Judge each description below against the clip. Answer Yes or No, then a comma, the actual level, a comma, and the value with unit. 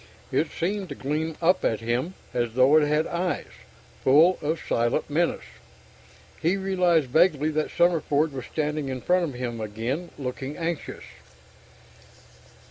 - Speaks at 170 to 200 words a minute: No, average, 140 wpm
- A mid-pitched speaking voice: Yes, medium, 150 Hz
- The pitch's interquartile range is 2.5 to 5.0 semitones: Yes, average, 4.7 semitones